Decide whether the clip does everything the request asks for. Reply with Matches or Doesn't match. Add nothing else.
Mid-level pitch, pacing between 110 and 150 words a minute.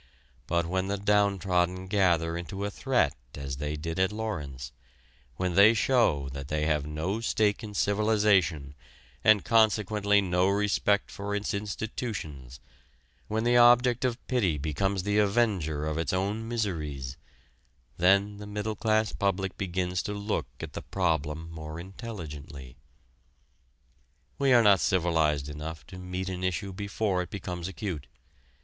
Doesn't match